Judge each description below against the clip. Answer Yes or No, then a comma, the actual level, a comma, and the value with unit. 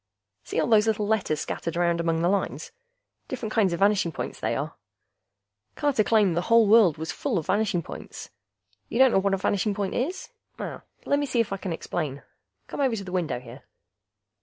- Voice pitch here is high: Yes, high, 200 Hz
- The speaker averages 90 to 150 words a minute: No, average, 195 wpm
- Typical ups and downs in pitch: Yes, average, 4.6 semitones